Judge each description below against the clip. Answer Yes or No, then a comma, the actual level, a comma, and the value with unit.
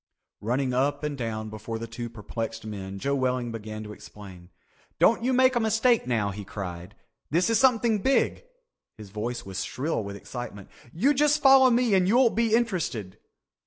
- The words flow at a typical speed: Yes, average, 170 wpm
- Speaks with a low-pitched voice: Yes, low, 125 Hz